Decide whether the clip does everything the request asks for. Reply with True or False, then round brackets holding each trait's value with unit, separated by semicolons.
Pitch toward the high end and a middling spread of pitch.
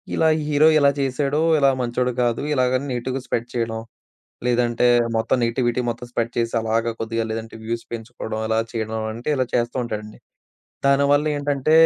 False (120 Hz; 3.0 semitones)